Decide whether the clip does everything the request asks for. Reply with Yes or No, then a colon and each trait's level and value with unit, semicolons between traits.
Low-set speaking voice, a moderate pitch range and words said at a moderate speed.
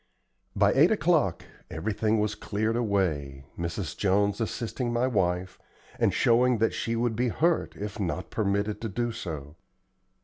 Yes: low, 105 Hz; average, 3.8 semitones; average, 145 wpm